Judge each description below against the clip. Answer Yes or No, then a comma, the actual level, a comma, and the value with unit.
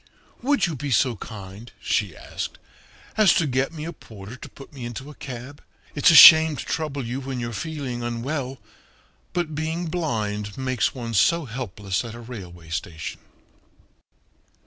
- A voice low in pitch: Yes, low, 130 Hz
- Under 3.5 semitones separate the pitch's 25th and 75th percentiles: No, average, 5.3 semitones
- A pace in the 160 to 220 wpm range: Yes, average, 165 wpm